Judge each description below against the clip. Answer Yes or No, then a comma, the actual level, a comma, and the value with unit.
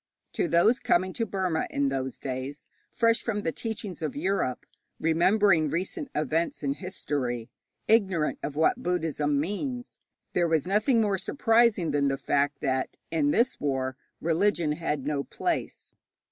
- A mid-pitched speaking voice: Yes, medium, 165 Hz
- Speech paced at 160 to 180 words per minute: No, average, 145 wpm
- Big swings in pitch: Yes, wide, 6.0 semitones